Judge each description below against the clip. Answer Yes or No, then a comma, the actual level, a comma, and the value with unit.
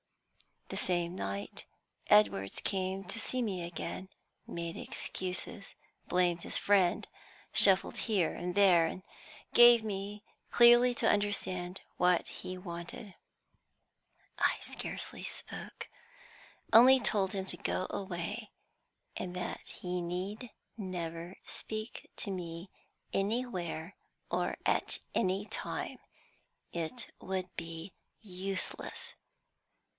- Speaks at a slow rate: Yes, slow, 105 wpm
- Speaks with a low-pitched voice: No, medium, 185 Hz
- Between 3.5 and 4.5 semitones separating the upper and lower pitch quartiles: No, average, 2.8 semitones